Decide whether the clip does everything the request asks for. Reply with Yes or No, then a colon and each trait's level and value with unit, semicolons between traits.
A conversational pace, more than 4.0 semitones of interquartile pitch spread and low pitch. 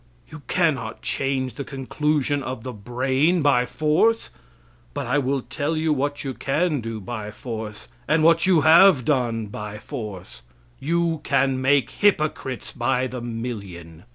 Yes: average, 150 wpm; average, 4.4 semitones; low, 130 Hz